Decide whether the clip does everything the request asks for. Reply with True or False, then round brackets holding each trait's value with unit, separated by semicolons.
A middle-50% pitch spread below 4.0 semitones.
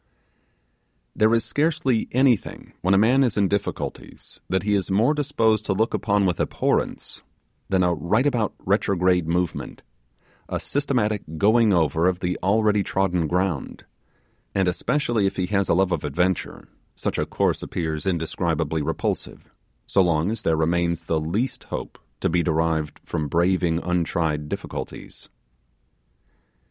False (4.3 semitones)